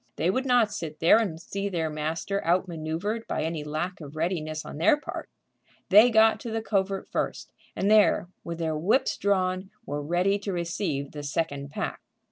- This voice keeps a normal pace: Yes, average, 180 wpm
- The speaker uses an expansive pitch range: No, average, 4.3 semitones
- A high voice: No, medium, 175 Hz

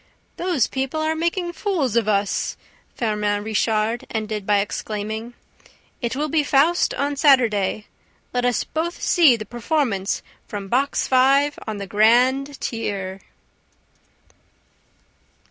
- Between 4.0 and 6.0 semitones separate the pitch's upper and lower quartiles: Yes, average, 5.3 semitones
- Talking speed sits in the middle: No, slow, 125 wpm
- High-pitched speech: Yes, high, 240 Hz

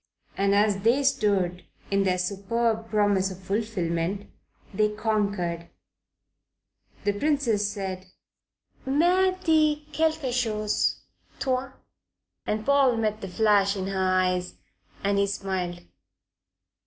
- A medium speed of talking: No, slow, 110 wpm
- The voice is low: No, high, 205 Hz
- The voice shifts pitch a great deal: No, average, 3.4 semitones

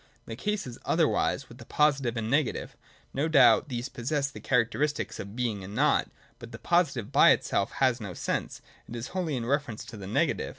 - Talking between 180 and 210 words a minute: Yes, fast, 205 wpm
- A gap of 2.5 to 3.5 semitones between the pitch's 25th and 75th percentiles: No, average, 4.2 semitones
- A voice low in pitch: Yes, low, 125 Hz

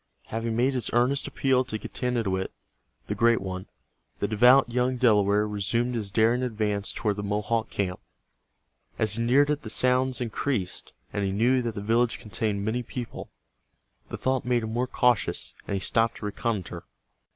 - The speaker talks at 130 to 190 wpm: Yes, average, 170 wpm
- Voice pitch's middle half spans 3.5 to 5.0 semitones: No, average, 3.1 semitones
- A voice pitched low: Yes, low, 115 Hz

